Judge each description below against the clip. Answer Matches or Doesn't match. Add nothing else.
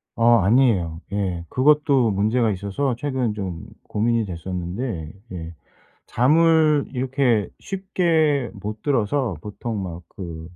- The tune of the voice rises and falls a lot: Matches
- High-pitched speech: Doesn't match